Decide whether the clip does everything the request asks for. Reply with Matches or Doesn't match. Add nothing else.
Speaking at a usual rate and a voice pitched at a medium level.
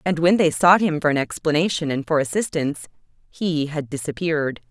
Matches